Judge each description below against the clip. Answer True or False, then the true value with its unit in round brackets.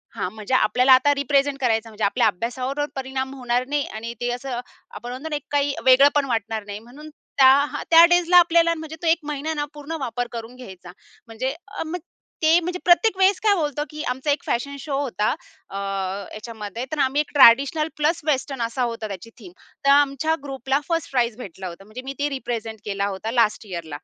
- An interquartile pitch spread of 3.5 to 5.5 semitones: True (4.6 semitones)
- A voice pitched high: True (260 Hz)